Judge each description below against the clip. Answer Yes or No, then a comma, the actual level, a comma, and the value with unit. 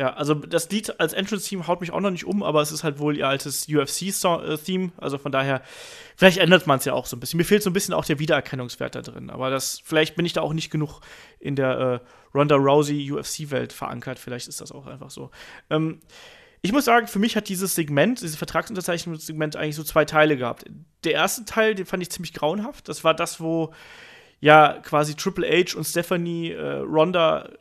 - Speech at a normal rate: No, fast, 220 wpm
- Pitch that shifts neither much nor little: Yes, average, 4.1 semitones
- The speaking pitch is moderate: Yes, medium, 160 Hz